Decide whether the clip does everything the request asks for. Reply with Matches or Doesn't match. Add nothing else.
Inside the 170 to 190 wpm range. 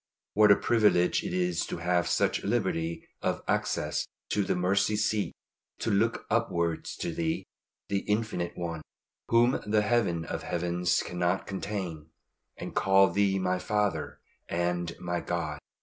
Doesn't match